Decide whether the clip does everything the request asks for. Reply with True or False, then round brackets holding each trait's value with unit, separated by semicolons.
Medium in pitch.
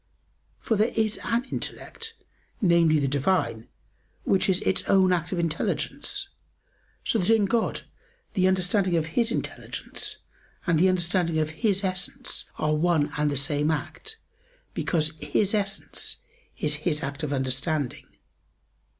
True (175 Hz)